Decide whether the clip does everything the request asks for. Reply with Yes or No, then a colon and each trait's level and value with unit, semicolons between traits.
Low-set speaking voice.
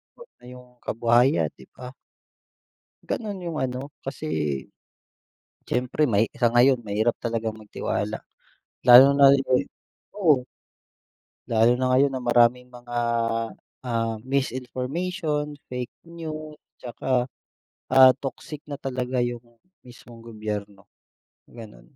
Yes: low, 125 Hz